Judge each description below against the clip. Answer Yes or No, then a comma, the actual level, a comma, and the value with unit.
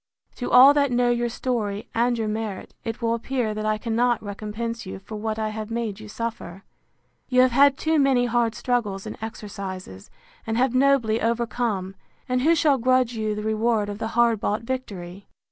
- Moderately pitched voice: No, high, 230 Hz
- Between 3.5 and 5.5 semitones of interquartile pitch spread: No, narrow, 2.5 semitones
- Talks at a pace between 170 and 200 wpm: Yes, average, 190 wpm